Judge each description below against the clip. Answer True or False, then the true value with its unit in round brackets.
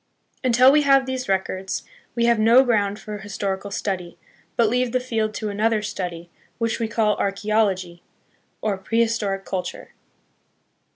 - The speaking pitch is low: False (215 Hz)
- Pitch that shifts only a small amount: False (3.2 semitones)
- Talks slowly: False (150 wpm)